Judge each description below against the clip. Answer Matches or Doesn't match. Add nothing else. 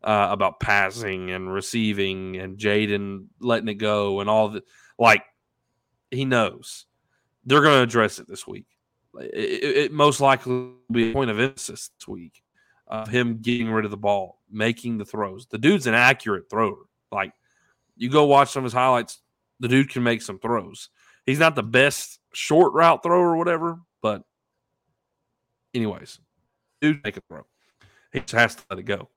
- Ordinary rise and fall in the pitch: Matches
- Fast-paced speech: Doesn't match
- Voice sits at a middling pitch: Doesn't match